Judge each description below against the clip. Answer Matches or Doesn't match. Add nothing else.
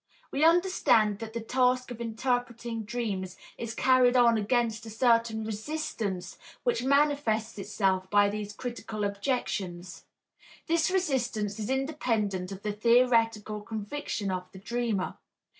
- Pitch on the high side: Matches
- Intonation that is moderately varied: Matches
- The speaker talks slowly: Matches